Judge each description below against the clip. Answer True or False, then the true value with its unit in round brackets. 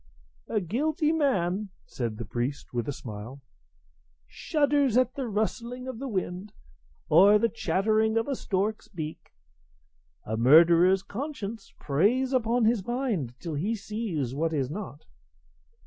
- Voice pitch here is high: True (205 Hz)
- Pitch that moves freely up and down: True (7.3 semitones)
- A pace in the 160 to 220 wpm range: False (135 wpm)